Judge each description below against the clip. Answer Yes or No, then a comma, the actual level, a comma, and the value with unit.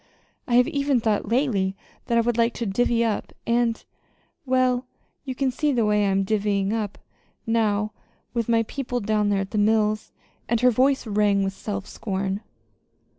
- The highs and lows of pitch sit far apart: No, average, 2.9 semitones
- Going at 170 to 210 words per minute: Yes, average, 180 wpm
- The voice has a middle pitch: No, high, 225 Hz